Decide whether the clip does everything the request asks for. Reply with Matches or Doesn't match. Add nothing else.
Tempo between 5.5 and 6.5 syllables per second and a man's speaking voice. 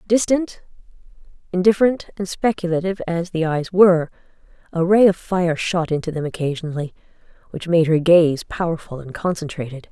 Doesn't match